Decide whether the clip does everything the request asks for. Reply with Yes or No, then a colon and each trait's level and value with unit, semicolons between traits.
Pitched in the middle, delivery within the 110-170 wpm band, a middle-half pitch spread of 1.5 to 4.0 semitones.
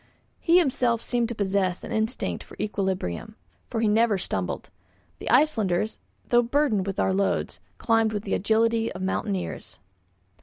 No: high, 220 Hz; average, 150 wpm; average, 3.3 semitones